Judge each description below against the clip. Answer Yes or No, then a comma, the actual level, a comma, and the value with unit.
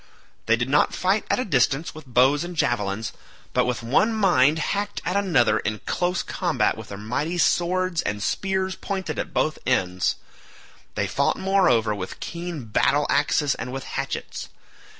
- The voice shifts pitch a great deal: Yes, wide, 7.6 semitones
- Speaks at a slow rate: No, average, 170 wpm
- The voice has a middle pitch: Yes, medium, 145 Hz